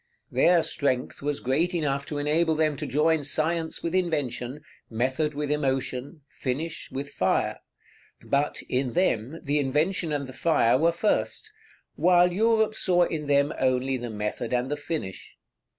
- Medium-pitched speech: Yes, medium, 150 Hz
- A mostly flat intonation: No, average, 3.9 semitones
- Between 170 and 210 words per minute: No, average, 150 wpm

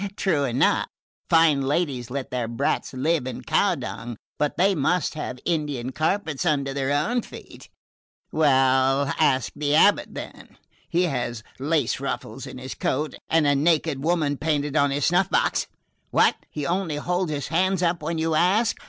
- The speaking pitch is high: No, medium, 150 Hz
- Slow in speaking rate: No, average, 165 wpm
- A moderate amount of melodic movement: Yes, average, 3.7 semitones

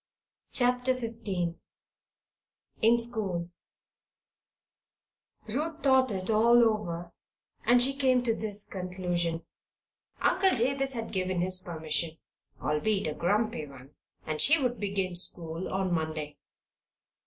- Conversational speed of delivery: No, slow, 110 wpm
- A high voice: Yes, high, 200 Hz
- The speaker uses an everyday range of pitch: No, wide, 5.8 semitones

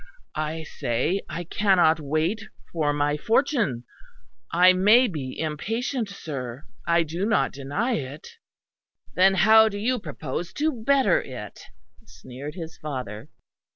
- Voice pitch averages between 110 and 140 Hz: No, medium, 170 Hz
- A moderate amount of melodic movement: No, wide, 6.6 semitones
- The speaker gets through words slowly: Yes, slow, 125 wpm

